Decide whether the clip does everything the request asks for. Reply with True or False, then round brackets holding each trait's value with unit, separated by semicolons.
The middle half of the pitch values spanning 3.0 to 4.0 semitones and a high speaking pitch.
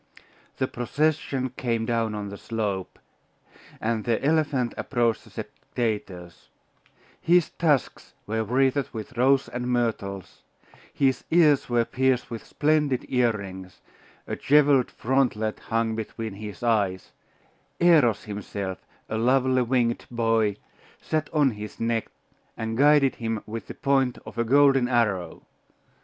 False (3.5 semitones; 120 Hz)